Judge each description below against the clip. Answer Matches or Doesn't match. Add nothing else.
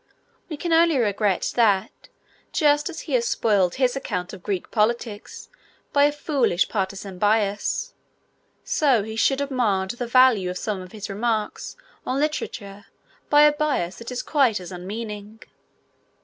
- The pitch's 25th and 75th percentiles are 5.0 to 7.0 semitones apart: Matches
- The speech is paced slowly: Doesn't match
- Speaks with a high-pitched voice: Matches